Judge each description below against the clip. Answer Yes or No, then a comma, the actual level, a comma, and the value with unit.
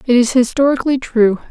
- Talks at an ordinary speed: Yes, average, 160 wpm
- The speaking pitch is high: Yes, very high, 250 Hz